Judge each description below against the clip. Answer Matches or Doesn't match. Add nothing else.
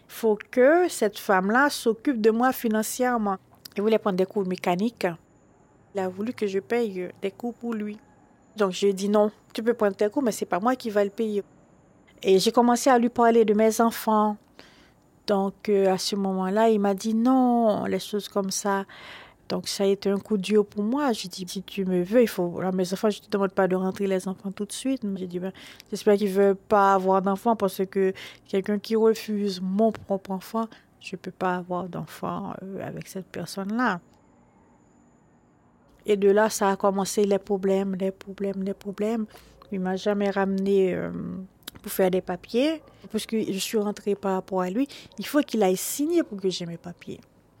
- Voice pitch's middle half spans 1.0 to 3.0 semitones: Matches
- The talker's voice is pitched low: Doesn't match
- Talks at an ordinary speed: Matches